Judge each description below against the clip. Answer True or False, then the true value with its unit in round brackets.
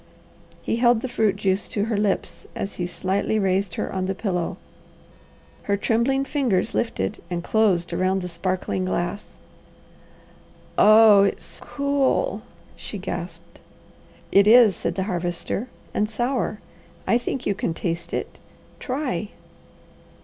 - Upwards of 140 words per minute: False (135 wpm)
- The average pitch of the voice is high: True (200 Hz)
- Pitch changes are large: False (3.9 semitones)